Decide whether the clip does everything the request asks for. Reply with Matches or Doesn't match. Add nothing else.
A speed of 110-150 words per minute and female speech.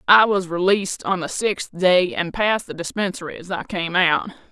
Doesn't match